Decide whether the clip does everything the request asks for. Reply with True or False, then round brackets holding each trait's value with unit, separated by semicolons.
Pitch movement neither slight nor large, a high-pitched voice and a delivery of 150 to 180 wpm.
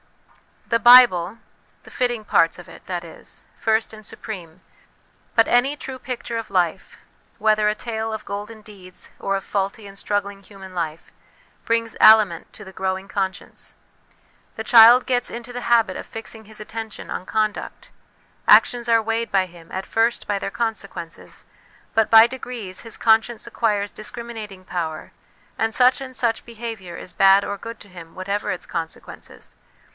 True (3.2 semitones; 215 Hz; 165 wpm)